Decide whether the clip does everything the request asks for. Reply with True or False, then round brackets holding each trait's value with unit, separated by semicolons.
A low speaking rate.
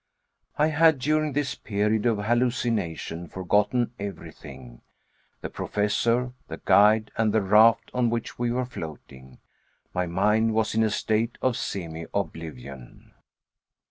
True (125 wpm)